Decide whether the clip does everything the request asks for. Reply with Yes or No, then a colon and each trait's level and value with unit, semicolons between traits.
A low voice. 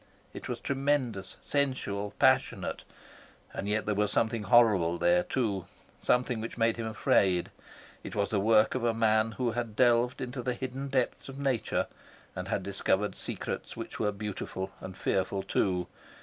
Yes: low, 110 Hz